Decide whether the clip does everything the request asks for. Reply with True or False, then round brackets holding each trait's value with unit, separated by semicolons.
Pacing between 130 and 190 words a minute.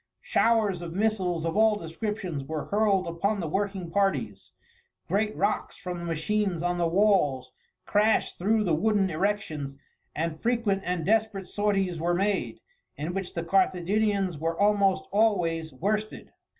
True (145 wpm)